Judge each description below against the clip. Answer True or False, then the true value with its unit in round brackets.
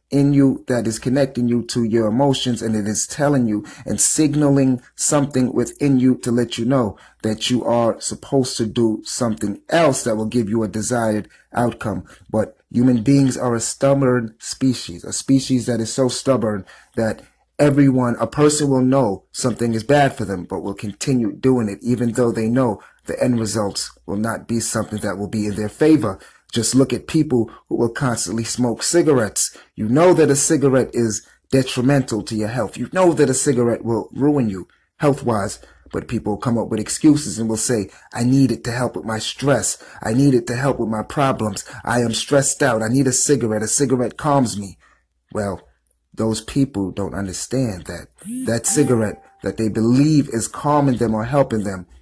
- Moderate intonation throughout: True (3.6 semitones)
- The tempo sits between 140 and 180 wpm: False (195 wpm)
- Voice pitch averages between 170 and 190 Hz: False (120 Hz)